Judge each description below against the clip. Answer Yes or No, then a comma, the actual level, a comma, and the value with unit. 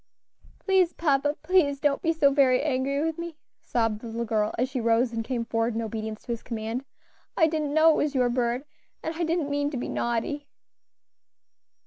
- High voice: Yes, very high, 270 Hz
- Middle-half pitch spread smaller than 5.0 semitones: Yes, average, 4.6 semitones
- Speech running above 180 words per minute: Yes, average, 195 wpm